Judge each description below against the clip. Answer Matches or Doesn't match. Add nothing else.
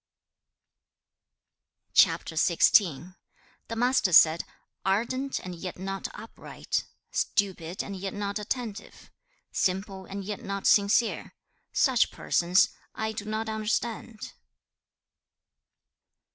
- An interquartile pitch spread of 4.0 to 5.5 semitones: Doesn't match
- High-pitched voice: Matches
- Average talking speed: Doesn't match